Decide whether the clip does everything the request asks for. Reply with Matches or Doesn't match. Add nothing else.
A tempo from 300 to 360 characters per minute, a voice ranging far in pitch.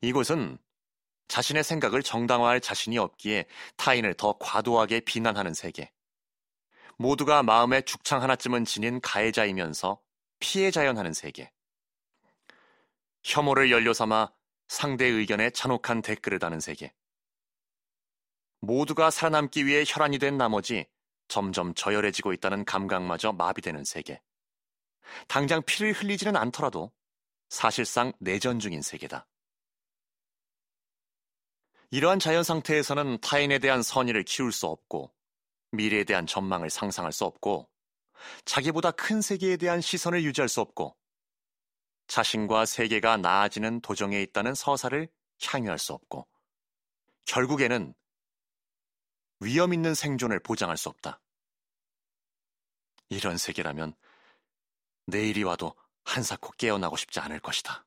Doesn't match